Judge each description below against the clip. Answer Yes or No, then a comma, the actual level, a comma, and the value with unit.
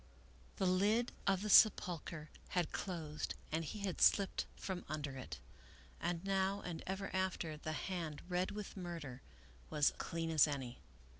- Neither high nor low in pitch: Yes, medium, 175 Hz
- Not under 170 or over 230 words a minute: No, average, 150 wpm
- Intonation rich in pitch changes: No, average, 3.8 semitones